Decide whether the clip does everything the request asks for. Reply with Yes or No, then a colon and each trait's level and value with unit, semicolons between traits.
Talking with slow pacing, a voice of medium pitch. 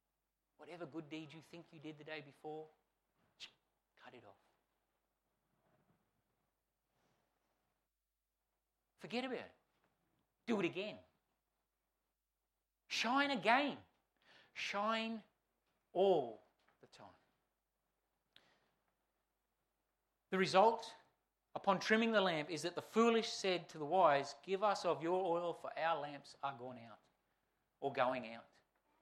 Yes: slow, 110 wpm; medium, 170 Hz